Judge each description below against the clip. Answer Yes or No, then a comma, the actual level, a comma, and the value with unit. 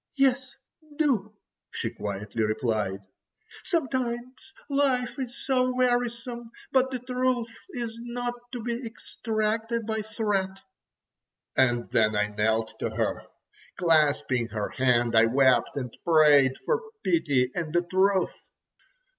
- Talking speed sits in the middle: No, slow, 120 wpm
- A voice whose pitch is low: No, high, 215 Hz